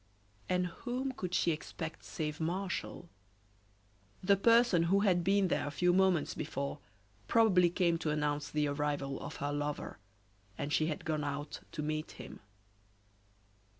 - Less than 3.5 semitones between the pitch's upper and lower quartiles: No, average, 3.9 semitones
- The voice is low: No, medium, 165 Hz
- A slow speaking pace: No, average, 150 wpm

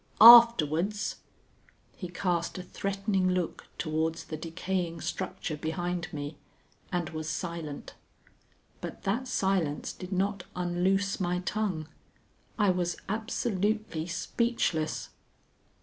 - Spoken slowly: Yes, slow, 105 wpm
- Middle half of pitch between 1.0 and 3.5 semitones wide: Yes, average, 3.2 semitones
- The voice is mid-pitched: Yes, medium, 180 Hz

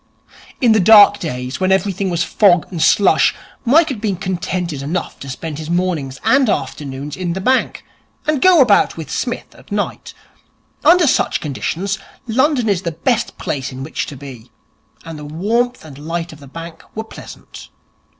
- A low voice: No, medium, 180 Hz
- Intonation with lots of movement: Yes, wide, 6.6 semitones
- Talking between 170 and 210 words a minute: Yes, average, 175 wpm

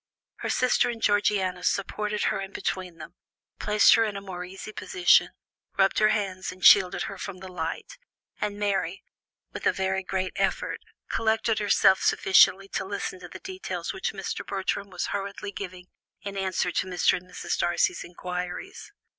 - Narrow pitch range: Yes, narrow, 2.1 semitones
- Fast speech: No, average, 170 wpm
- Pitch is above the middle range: Yes, high, 195 Hz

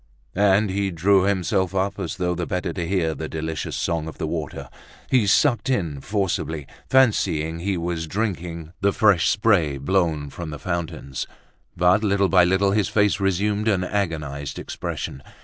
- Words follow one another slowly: No, average, 165 wpm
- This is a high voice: No, very low, 90 Hz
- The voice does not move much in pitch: No, average, 3.6 semitones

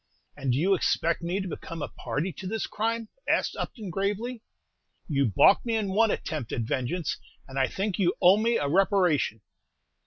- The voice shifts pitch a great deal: Yes, wide, 6.2 semitones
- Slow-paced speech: No, average, 185 wpm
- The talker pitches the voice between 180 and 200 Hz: Yes, medium, 185 Hz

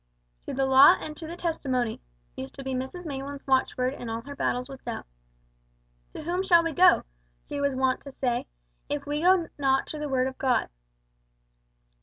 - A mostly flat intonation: No, average, 3.0 semitones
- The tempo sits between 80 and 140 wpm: No, average, 190 wpm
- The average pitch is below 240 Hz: No, very high, 275 Hz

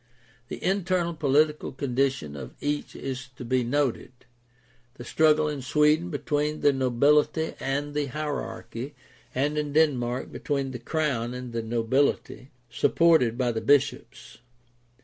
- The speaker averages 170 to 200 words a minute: No, slow, 135 wpm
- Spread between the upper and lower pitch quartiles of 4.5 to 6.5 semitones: No, average, 3.2 semitones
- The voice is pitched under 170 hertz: Yes, medium, 140 Hz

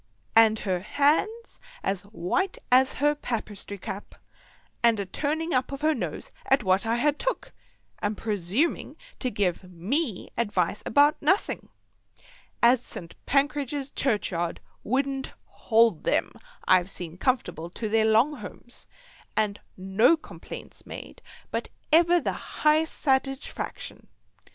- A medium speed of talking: No, slow, 130 wpm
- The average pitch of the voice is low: No, high, 235 Hz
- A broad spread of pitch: Yes, wide, 6.4 semitones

